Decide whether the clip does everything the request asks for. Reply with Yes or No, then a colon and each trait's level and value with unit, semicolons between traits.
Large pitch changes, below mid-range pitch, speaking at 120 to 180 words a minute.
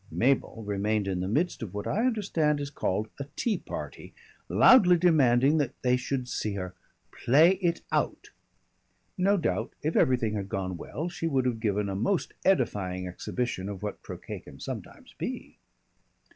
Yes: wide, 7.8 semitones; low, 125 Hz; average, 165 wpm